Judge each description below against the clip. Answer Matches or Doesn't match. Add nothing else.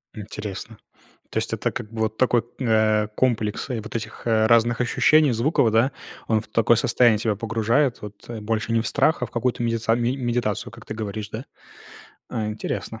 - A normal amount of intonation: Doesn't match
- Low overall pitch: Matches